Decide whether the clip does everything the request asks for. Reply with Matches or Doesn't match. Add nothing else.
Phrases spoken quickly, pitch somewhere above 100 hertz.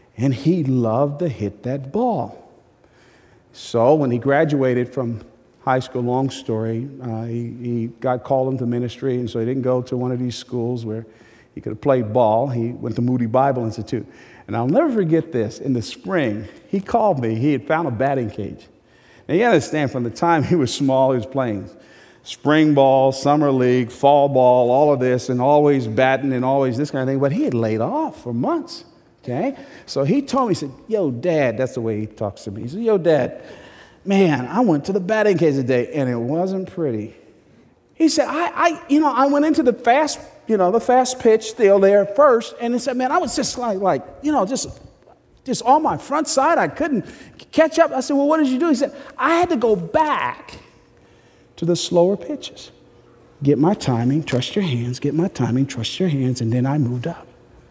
Matches